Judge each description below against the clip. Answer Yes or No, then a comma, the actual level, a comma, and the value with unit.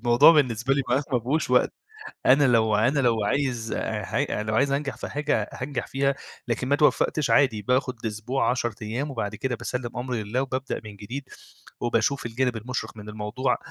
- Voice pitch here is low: Yes, low, 125 Hz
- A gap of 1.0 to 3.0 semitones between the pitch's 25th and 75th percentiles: No, average, 3.4 semitones